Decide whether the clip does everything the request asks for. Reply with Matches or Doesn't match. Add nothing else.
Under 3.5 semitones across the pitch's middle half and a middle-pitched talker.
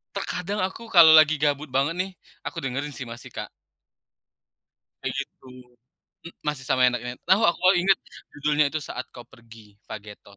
Doesn't match